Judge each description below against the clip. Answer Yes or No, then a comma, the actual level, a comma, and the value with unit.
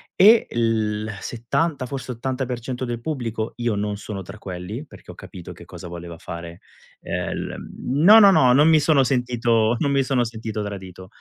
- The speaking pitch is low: Yes, low, 120 Hz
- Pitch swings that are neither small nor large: Yes, average, 4.3 semitones